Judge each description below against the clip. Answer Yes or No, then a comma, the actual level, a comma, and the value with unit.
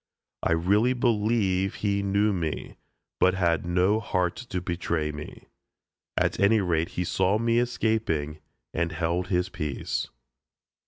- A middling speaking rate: No, slow, 130 wpm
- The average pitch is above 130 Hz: No, very low, 95 Hz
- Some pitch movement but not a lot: Yes, average, 3.8 semitones